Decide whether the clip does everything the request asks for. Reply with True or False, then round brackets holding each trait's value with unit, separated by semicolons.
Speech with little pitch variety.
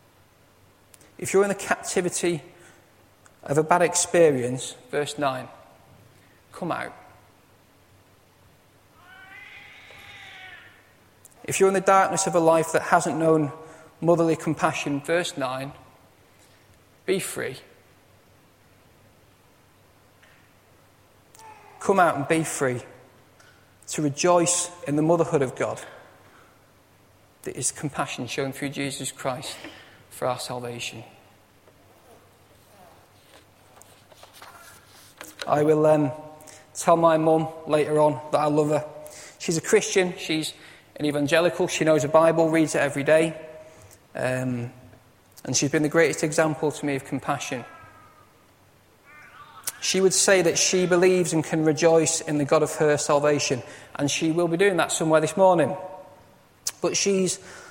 False (4.5 semitones)